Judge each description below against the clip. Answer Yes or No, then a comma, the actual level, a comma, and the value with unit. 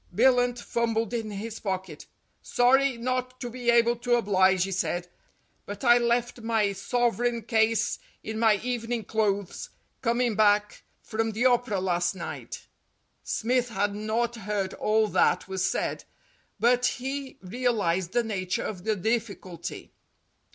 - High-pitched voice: Yes, high, 225 Hz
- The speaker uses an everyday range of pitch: Yes, average, 3.2 semitones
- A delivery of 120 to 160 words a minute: Yes, average, 140 wpm